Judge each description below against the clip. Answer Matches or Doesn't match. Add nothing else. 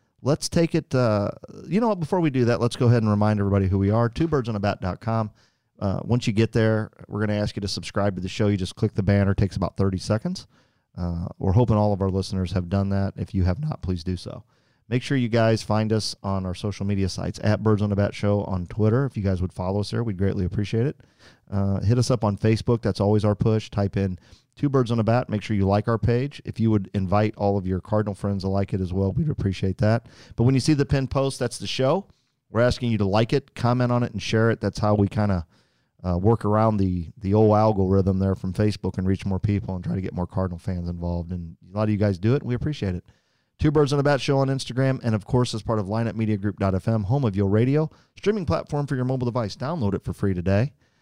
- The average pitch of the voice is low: Matches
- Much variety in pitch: Doesn't match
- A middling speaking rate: Doesn't match